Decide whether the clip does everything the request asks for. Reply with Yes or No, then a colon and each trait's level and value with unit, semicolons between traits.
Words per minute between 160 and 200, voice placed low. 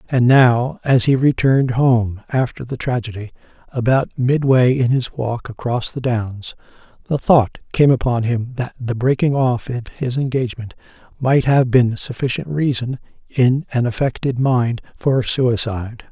No: average, 150 wpm; low, 125 Hz